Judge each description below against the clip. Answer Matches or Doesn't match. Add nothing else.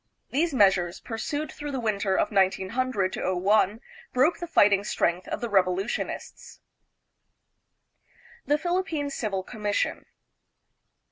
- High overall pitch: Matches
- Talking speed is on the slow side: Matches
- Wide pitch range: Matches